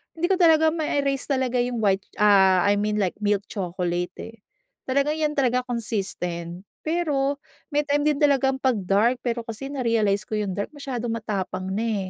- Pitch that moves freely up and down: Yes, wide, 5.7 semitones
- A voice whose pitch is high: Yes, high, 230 Hz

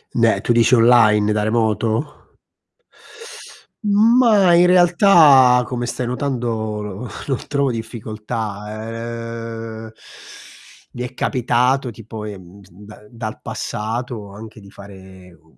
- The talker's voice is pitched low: Yes, low, 115 Hz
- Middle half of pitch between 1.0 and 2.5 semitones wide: No, average, 2.9 semitones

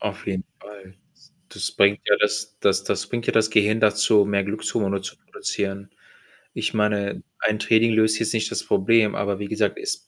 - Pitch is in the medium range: No, low, 105 Hz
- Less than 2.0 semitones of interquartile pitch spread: Yes, narrow, 1.6 semitones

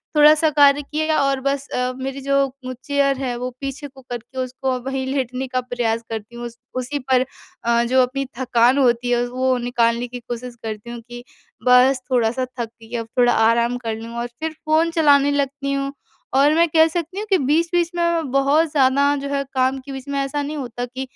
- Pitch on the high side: Yes, very high, 265 Hz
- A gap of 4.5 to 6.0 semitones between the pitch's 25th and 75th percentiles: No, narrow, 2.6 semitones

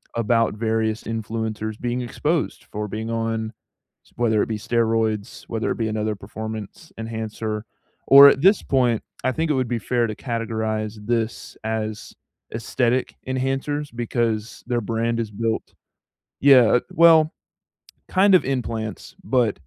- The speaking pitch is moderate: No, low, 115 Hz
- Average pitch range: No, narrow, 2.2 semitones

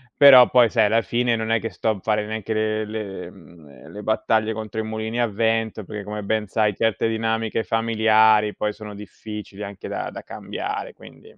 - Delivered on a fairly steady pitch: Yes, narrow, 1.3 semitones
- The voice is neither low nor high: No, low, 110 Hz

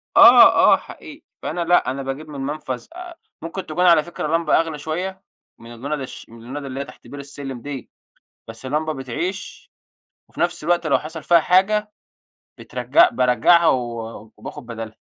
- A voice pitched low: No, medium, 155 Hz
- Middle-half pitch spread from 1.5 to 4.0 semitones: No, average, 4.5 semitones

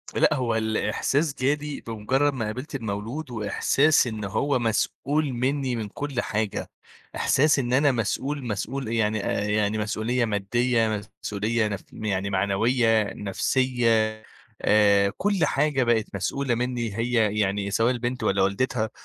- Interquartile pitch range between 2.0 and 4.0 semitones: Yes, average, 3.6 semitones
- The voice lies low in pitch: Yes, low, 115 Hz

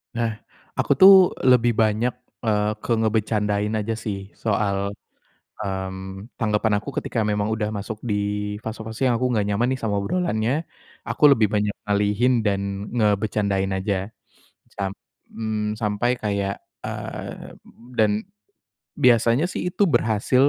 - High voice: No, low, 105 Hz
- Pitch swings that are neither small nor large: No, narrow, 1.9 semitones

